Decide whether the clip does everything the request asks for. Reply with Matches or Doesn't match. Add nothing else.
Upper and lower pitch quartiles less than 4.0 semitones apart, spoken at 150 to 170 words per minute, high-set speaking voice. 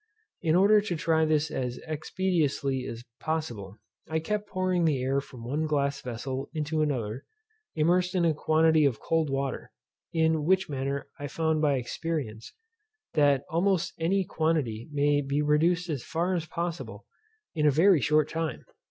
Doesn't match